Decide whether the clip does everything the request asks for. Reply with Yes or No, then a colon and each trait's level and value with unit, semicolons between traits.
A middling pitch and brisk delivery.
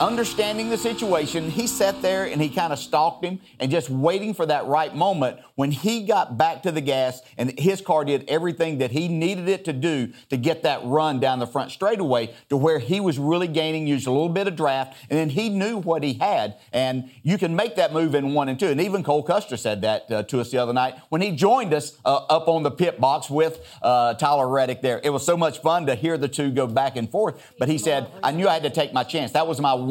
Yes: medium, 155 Hz; fast, 255 wpm